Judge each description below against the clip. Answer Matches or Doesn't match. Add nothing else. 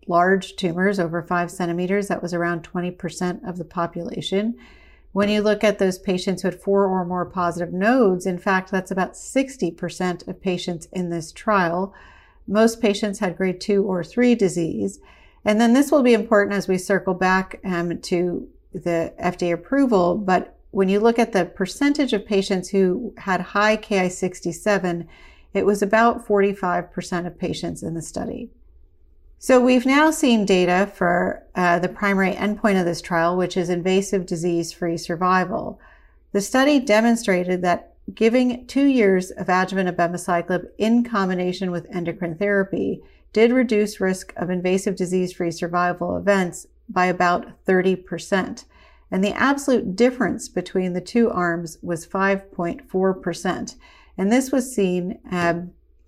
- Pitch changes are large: Doesn't match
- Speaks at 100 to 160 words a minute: Matches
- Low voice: Doesn't match